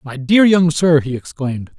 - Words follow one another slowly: No, average, 200 wpm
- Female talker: No, male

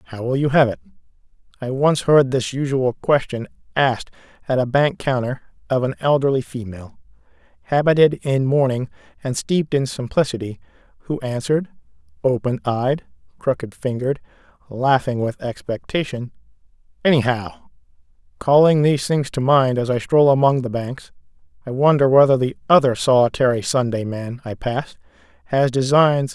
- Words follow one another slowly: No, average, 145 wpm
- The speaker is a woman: No, male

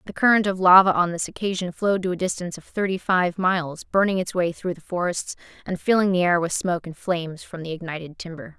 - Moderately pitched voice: Yes, medium, 180 Hz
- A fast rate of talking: Yes, fast, 230 wpm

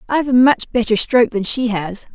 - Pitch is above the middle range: Yes, high, 230 Hz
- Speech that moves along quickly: Yes, fast, 225 wpm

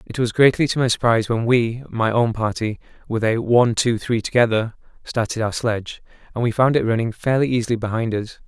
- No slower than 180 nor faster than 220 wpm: Yes, average, 190 wpm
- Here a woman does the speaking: No, male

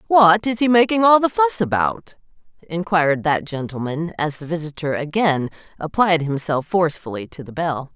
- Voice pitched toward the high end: No, medium, 170 Hz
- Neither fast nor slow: Yes, average, 160 wpm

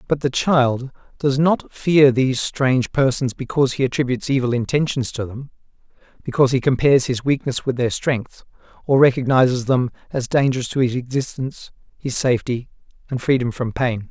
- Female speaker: No, male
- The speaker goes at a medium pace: Yes, average, 160 wpm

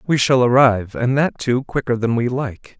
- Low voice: Yes, low, 125 Hz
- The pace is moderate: No, fast, 215 wpm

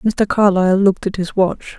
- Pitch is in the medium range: No, high, 195 Hz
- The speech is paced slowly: No, average, 200 wpm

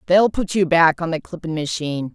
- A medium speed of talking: Yes, average, 195 wpm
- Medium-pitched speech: Yes, medium, 170 Hz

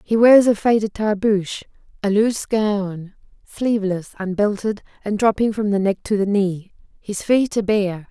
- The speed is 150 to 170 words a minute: Yes, average, 165 wpm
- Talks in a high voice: Yes, high, 205 Hz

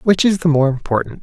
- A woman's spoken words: No, male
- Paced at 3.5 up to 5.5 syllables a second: No, 5.9 syllables/s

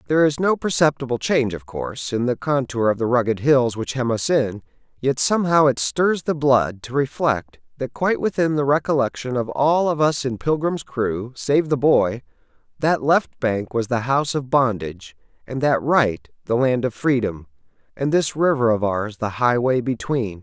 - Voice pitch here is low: Yes, low, 130 Hz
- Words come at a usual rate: Yes, average, 190 wpm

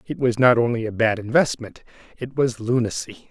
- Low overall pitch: Yes, low, 120 Hz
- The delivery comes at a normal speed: Yes, average, 180 wpm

